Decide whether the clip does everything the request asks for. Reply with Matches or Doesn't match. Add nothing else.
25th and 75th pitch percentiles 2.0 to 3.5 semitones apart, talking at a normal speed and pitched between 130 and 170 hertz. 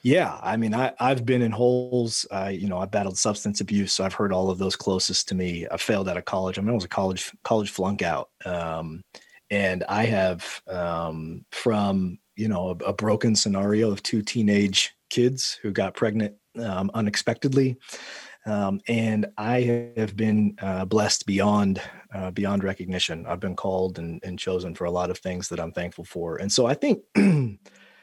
Doesn't match